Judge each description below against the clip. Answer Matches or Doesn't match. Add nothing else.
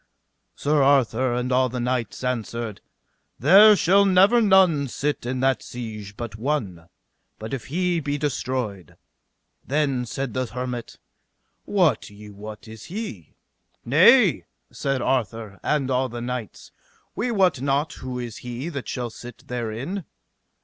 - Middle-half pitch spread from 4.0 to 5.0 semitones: Matches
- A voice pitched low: Matches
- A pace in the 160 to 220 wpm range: Doesn't match